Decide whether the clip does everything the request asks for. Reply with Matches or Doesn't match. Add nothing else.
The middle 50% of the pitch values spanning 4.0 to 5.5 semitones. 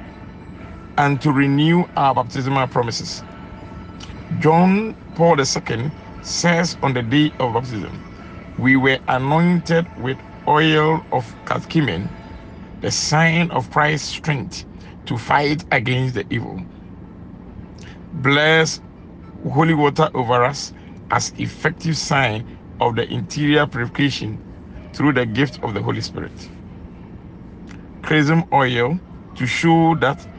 Matches